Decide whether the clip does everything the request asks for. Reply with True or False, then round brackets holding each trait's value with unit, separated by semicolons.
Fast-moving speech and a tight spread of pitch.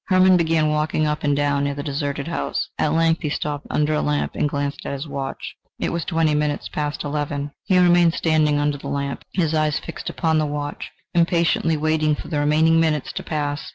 True (210 wpm; 1.9 semitones)